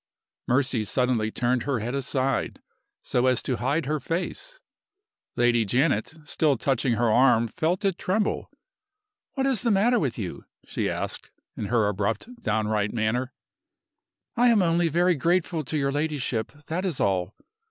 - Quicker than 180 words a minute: No, average, 150 wpm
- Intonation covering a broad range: Yes, wide, 6.3 semitones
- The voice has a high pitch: No, low, 135 Hz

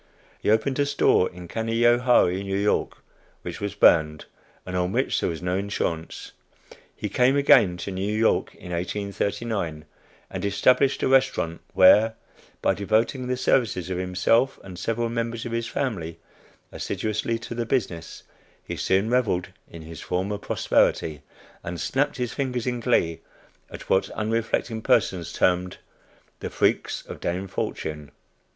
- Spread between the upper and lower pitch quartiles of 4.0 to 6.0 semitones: Yes, average, 4.7 semitones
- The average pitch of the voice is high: No, low, 105 Hz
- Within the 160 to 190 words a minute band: No, average, 145 wpm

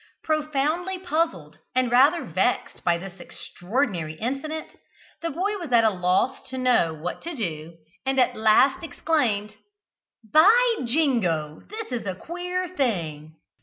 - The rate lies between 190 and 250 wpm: No, slow, 135 wpm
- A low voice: No, very high, 255 Hz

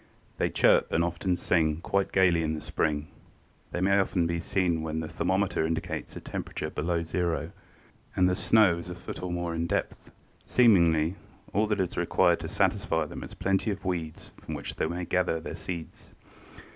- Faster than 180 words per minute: Yes, average, 190 wpm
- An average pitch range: No, narrow, 2.3 semitones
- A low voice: Yes, very low, 85 Hz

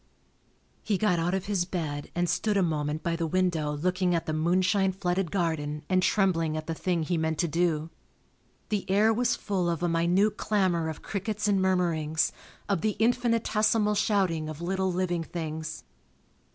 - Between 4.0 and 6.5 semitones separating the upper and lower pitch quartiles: No, average, 3.2 semitones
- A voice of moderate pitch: Yes, medium, 175 Hz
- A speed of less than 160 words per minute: No, average, 175 wpm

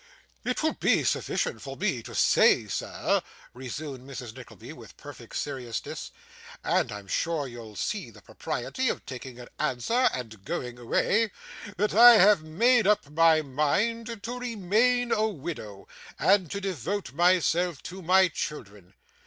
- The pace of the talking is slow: No, average, 145 wpm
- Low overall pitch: No, medium, 165 Hz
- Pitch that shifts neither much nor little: No, wide, 8.8 semitones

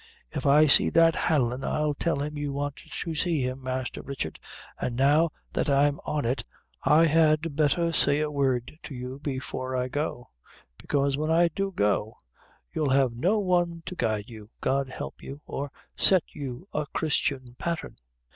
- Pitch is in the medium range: Yes, medium, 145 Hz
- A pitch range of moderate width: Yes, average, 3.5 semitones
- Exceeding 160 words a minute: Yes, average, 175 wpm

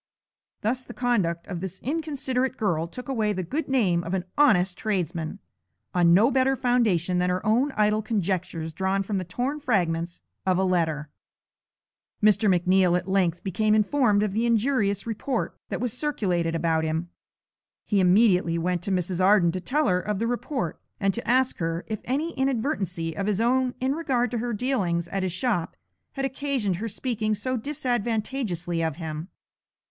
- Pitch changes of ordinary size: No, wide, 5.8 semitones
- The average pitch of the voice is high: Yes, high, 205 Hz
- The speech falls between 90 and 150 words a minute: No, average, 175 wpm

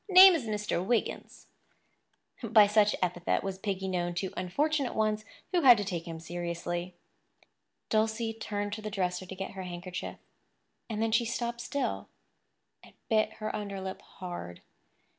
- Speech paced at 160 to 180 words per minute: No, average, 150 wpm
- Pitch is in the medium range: No, high, 205 Hz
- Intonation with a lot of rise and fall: No, average, 3.6 semitones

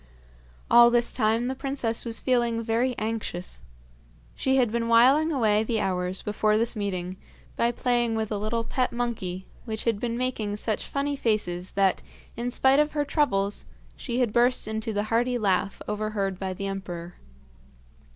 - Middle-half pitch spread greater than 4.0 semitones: No, average, 3.0 semitones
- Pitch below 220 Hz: No, high, 225 Hz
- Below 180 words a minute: Yes, average, 165 wpm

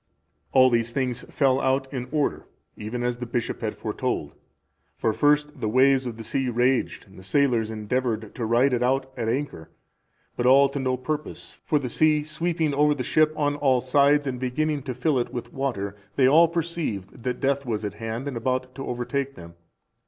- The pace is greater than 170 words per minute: Yes, average, 195 wpm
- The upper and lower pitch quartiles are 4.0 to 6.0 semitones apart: No, average, 3.0 semitones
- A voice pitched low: Yes, low, 130 Hz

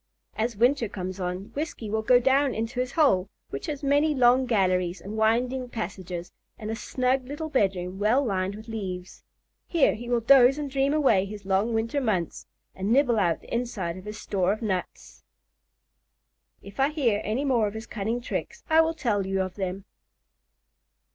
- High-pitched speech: Yes, high, 225 Hz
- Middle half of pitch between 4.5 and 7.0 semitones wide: Yes, average, 5.2 semitones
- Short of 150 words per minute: No, average, 180 wpm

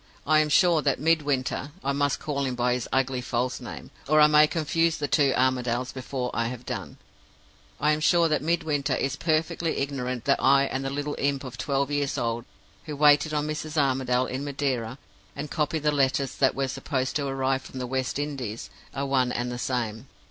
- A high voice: No, medium, 140 Hz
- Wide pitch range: No, narrow, 2.6 semitones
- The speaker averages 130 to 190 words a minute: No, average, 200 wpm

